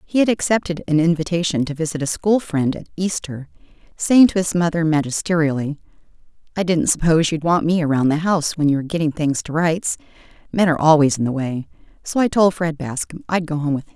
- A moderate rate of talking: No, fast, 210 wpm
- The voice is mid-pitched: Yes, medium, 165 Hz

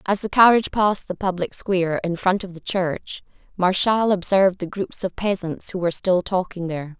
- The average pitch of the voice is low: No, medium, 185 Hz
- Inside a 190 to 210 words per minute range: Yes, average, 195 wpm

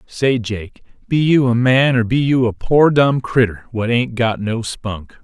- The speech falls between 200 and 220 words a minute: Yes, fast, 205 wpm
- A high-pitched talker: No, low, 120 Hz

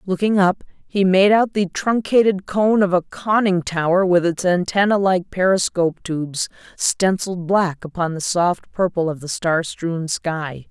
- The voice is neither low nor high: Yes, medium, 180 Hz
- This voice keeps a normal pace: Yes, average, 165 wpm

